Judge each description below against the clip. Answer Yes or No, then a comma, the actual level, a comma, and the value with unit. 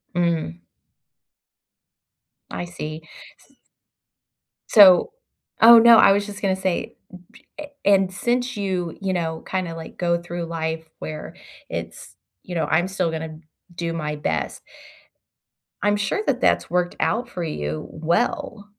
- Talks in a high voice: No, medium, 175 Hz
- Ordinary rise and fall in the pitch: Yes, average, 3.7 semitones